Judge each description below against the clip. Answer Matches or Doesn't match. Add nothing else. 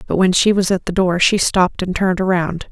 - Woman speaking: Matches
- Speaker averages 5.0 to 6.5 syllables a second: Matches